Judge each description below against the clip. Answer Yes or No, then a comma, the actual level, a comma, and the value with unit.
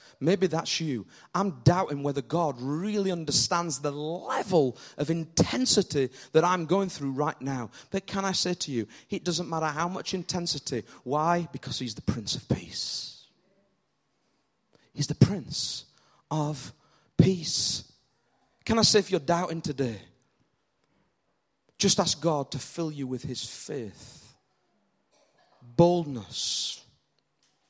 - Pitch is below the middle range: No, medium, 160 Hz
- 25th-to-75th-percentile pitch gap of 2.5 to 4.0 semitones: No, average, 4.6 semitones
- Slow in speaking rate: Yes, slow, 130 wpm